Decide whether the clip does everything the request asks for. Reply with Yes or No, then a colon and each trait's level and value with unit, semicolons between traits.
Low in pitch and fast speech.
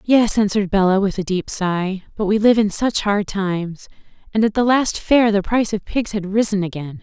No: high, 205 Hz; fast, 220 wpm